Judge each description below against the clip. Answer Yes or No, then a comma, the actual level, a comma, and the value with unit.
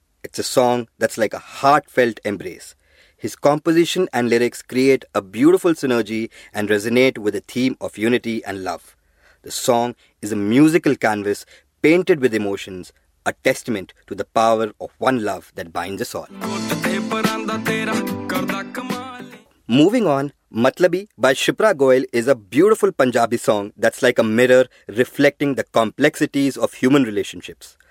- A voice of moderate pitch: No, low, 125 Hz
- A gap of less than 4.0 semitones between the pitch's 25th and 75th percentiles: No, average, 4.3 semitones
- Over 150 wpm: No, average, 145 wpm